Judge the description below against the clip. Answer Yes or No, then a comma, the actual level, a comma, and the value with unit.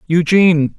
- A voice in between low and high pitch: Yes, medium, 165 Hz